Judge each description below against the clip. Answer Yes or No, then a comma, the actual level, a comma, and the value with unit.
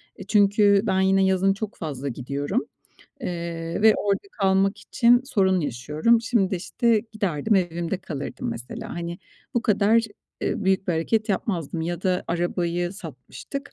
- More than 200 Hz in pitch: No, high, 190 Hz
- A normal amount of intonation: Yes, average, 3.6 semitones